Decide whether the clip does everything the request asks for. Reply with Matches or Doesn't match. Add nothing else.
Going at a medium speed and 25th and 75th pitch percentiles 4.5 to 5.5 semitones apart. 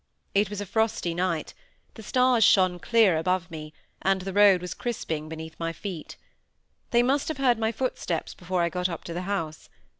Matches